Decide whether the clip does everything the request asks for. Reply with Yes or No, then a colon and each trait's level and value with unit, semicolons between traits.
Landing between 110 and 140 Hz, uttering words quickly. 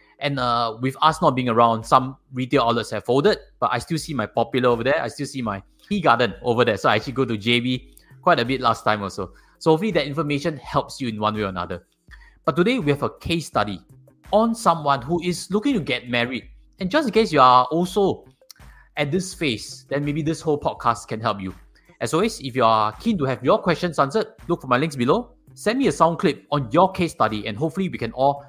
Yes: low, 135 Hz; fast, 240 wpm